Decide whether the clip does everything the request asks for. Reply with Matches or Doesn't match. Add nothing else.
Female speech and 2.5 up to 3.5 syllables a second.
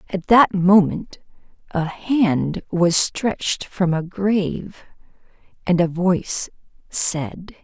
Matches